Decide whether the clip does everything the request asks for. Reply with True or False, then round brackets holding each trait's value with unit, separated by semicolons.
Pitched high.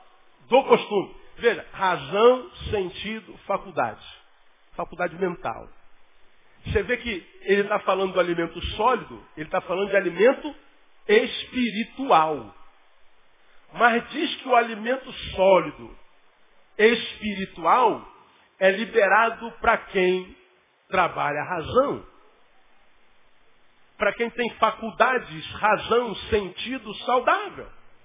True (215 Hz)